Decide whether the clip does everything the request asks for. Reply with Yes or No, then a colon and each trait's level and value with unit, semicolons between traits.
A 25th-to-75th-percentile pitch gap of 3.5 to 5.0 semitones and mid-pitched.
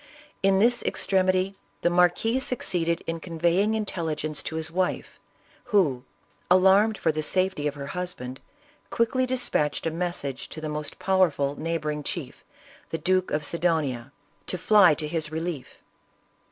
Yes: average, 3.8 semitones; medium, 170 Hz